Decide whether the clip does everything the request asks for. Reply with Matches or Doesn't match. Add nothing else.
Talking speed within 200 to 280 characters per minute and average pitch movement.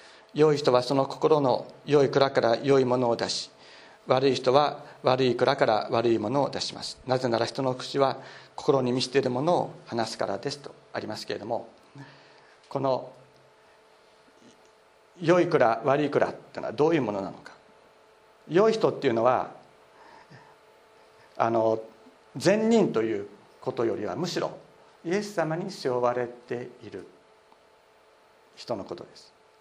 Matches